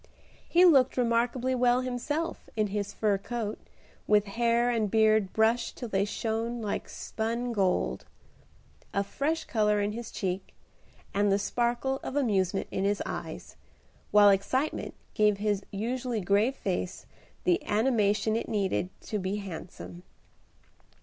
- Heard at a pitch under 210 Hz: No, high, 220 Hz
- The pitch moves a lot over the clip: No, average, 3.2 semitones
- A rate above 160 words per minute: No, slow, 135 wpm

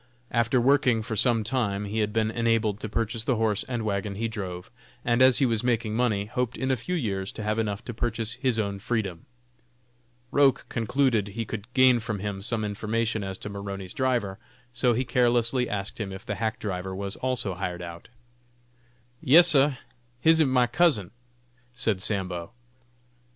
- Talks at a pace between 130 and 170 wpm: No, average, 180 wpm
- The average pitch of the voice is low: Yes, low, 110 Hz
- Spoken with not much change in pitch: No, average, 3.5 semitones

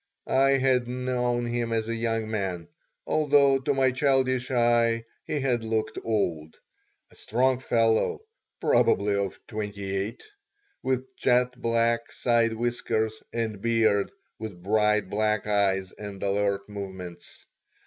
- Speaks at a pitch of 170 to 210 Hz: No, low, 115 Hz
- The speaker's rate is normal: No, slow, 130 wpm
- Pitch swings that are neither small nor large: Yes, average, 3.3 semitones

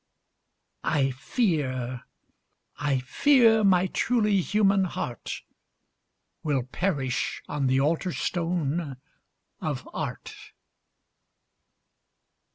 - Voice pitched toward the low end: No, medium, 160 Hz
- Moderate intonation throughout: No, wide, 6.7 semitones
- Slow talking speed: Yes, slow, 75 wpm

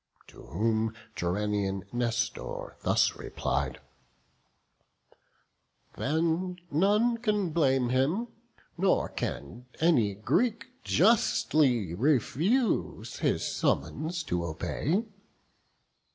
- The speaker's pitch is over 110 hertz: Yes, low, 135 Hz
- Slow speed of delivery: Yes, slow, 80 wpm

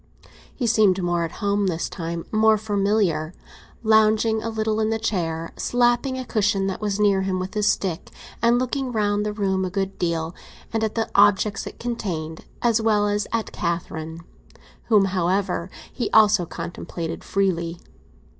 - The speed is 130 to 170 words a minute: Yes, average, 160 wpm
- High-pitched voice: Yes, high, 205 Hz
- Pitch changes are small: No, average, 3.7 semitones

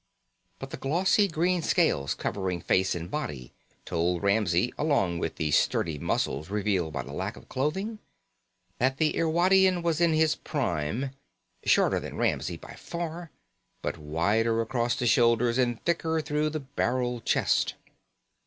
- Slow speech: No, average, 145 wpm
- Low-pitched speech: Yes, low, 120 Hz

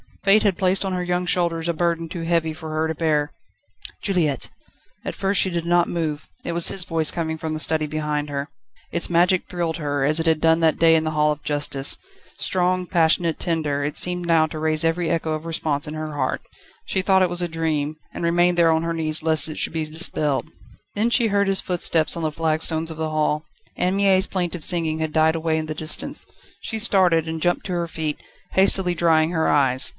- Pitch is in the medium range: Yes, medium, 165 Hz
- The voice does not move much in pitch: Yes, narrow, 2.1 semitones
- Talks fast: Yes, fast, 220 wpm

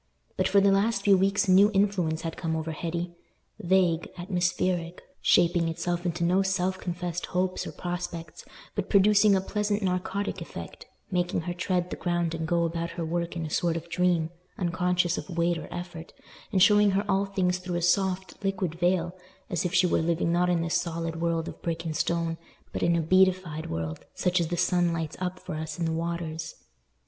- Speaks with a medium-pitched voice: Yes, medium, 175 Hz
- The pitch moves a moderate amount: No, narrow, 2.0 semitones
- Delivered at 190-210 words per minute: Yes, average, 195 wpm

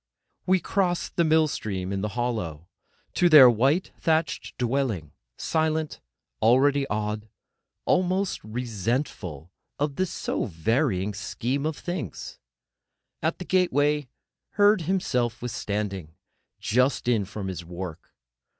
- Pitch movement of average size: No, wide, 7.5 semitones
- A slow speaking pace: Yes, slow, 115 wpm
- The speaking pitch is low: Yes, low, 125 Hz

